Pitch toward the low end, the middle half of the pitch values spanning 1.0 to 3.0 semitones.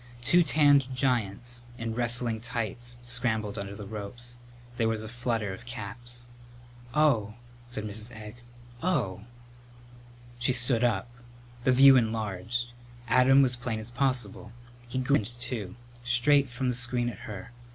Yes: low, 120 Hz; narrow, 2.4 semitones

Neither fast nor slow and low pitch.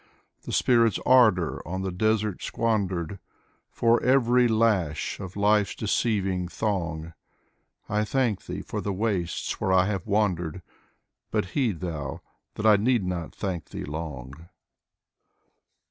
No: slow, 130 wpm; low, 100 Hz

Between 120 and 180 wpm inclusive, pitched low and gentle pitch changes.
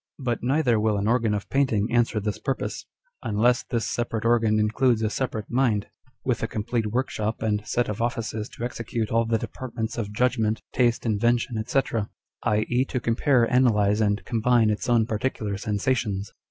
Yes: average, 165 wpm; low, 115 Hz; narrow, 2.3 semitones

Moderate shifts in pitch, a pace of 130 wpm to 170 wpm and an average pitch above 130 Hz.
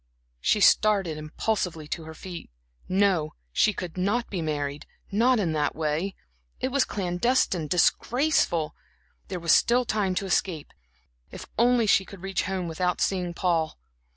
Yes: average, 4.4 semitones; average, 150 wpm; medium, 185 Hz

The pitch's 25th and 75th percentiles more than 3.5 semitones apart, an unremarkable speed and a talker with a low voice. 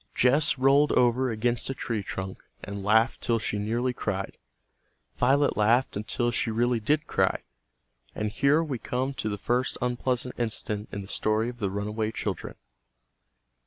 No: average, 3.2 semitones; average, 160 wpm; low, 120 Hz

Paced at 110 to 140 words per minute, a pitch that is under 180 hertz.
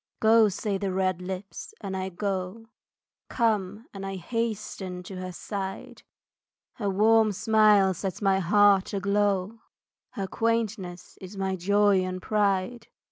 No: slow, 135 wpm; high, 195 Hz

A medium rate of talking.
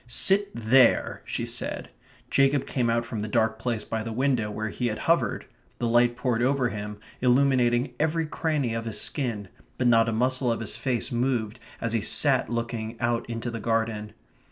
Yes: average, 185 wpm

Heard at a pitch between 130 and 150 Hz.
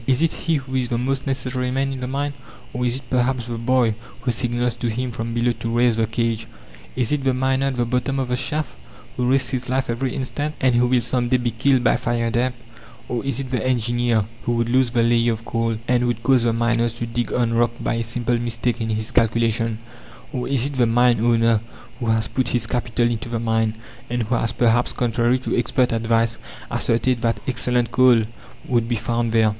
No: low, 120 Hz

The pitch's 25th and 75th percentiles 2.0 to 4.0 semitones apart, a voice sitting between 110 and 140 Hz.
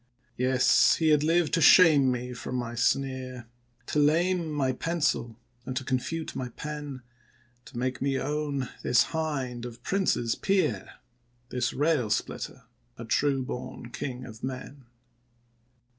Yes: average, 3.4 semitones; low, 135 Hz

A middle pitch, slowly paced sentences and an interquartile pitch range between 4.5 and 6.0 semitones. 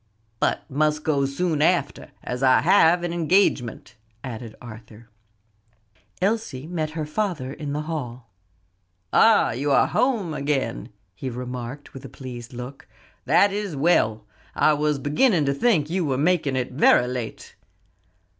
No: medium, 145 Hz; average, 145 wpm; average, 4.9 semitones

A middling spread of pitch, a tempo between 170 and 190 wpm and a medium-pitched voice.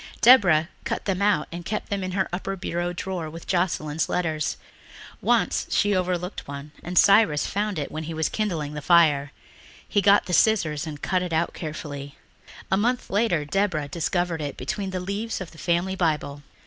Yes: average, 4.0 semitones; average, 185 wpm; medium, 175 Hz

